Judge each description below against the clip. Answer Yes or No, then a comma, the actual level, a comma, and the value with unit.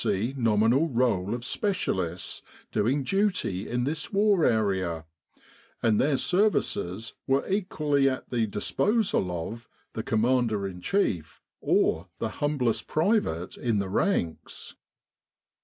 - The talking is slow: Yes, slow, 120 wpm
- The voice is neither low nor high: No, low, 120 Hz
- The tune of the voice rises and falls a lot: Yes, wide, 7.3 semitones